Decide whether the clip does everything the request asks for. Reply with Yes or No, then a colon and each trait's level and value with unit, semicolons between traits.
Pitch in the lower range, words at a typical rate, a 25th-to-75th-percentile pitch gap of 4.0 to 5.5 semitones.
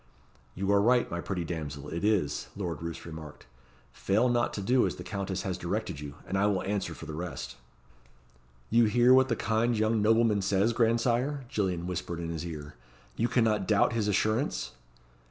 Yes: low, 100 Hz; average, 185 wpm; average, 5.2 semitones